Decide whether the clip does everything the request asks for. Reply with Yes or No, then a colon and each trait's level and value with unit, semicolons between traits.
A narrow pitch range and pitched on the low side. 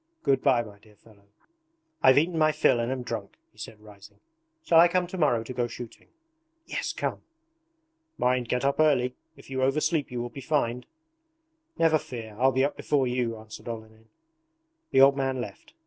No: average, 3.5 semitones; low, 125 Hz